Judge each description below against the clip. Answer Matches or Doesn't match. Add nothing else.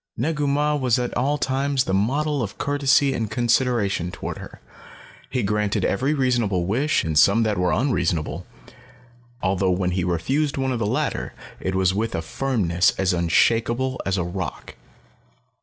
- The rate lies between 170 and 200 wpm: Doesn't match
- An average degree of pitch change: Doesn't match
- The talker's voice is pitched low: Matches